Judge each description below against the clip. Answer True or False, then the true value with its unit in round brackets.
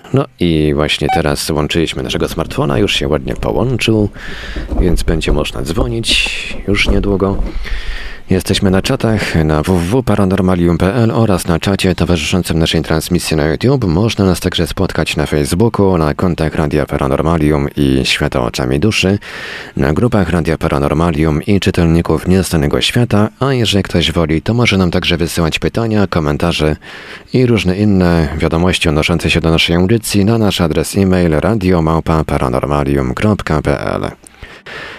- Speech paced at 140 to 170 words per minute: False (130 wpm)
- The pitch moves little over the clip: False (4.0 semitones)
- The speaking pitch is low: True (85 Hz)